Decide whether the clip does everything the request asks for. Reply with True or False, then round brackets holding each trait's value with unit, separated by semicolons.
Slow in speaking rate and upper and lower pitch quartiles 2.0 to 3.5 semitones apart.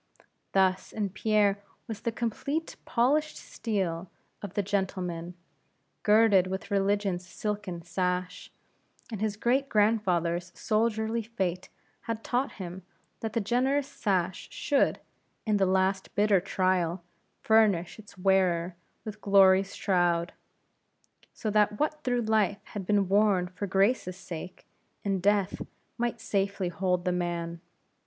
True (125 wpm; 3.0 semitones)